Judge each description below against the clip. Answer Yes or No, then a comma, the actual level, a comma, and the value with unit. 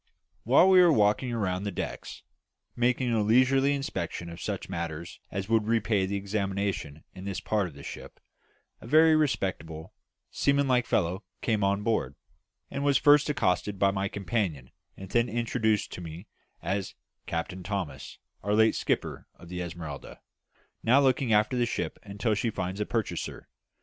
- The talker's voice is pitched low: Yes, low, 105 Hz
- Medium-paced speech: Yes, average, 160 wpm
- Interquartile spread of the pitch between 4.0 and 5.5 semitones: Yes, average, 4.7 semitones